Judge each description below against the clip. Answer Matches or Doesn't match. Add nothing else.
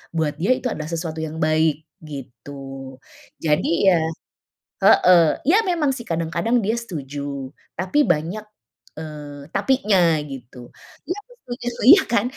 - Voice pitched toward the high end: Doesn't match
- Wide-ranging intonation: Matches